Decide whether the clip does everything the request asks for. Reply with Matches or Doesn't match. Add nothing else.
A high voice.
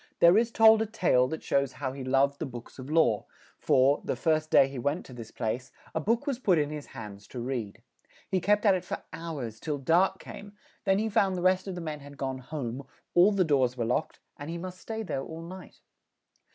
Doesn't match